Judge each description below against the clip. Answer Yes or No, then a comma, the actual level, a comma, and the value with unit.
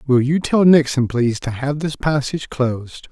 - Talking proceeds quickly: No, average, 190 wpm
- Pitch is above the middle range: No, low, 135 Hz